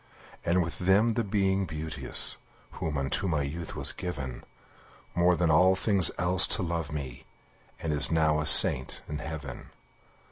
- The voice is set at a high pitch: No, very low, 80 Hz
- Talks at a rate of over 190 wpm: No, average, 155 wpm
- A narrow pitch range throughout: No, average, 3.4 semitones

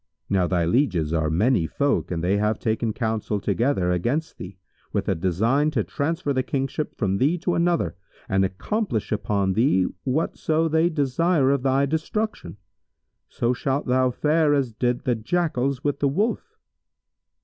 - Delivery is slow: No, average, 160 wpm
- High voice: No, low, 125 Hz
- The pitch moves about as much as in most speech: No, wide, 6.8 semitones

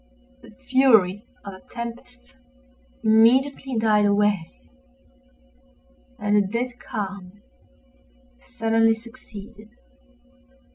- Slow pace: Yes, slow, 80 wpm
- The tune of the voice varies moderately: Yes, average, 3.1 semitones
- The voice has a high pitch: Yes, high, 225 Hz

